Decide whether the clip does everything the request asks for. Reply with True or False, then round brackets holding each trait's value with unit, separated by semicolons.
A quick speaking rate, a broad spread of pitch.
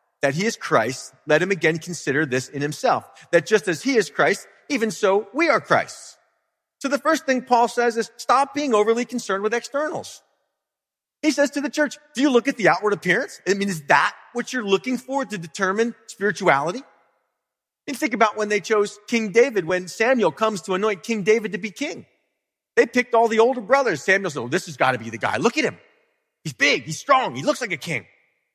True (225 wpm; 6.0 semitones)